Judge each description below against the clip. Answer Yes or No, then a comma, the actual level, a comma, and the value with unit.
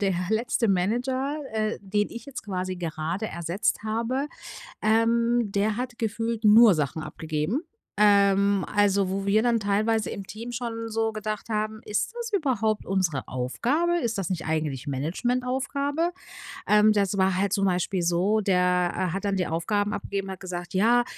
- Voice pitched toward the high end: Yes, high, 210 Hz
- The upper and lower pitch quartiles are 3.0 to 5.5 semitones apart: Yes, average, 3.7 semitones